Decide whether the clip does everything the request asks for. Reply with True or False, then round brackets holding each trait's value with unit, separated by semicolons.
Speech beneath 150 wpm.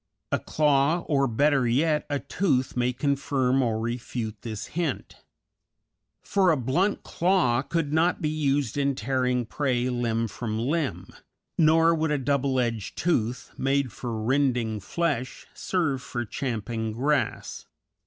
True (135 wpm)